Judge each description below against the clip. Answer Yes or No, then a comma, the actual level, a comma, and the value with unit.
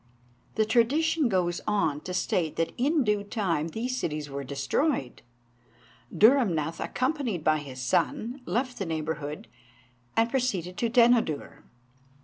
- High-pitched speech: Yes, high, 200 Hz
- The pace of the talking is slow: Yes, slow, 125 wpm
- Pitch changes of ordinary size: No, wide, 7.8 semitones